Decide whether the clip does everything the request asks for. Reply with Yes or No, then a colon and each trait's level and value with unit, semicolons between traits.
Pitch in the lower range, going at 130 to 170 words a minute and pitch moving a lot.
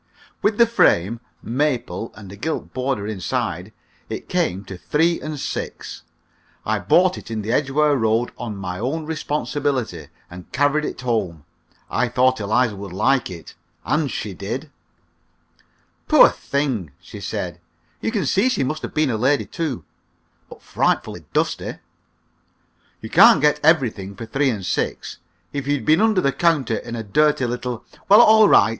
Yes: low, 130 Hz; average, 165 wpm; wide, 5.9 semitones